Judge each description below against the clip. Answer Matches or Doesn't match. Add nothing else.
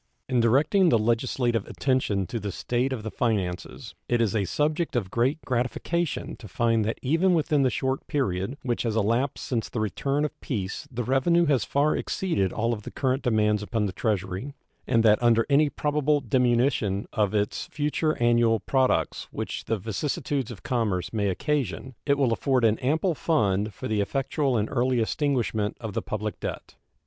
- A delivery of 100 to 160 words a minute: Doesn't match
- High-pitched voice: Doesn't match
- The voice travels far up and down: Doesn't match